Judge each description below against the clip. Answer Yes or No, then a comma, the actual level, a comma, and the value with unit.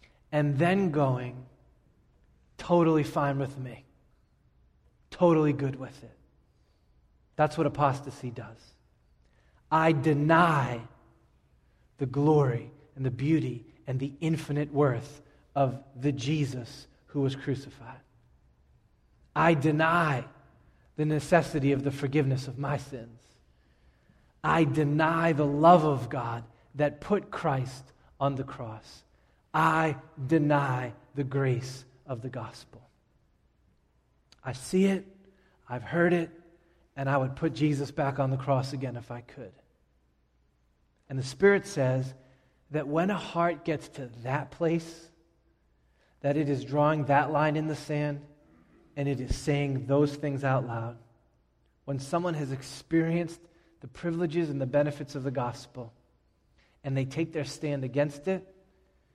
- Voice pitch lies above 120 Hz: Yes, medium, 140 Hz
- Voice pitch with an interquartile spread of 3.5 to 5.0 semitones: Yes, average, 4.0 semitones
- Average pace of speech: No, slow, 130 wpm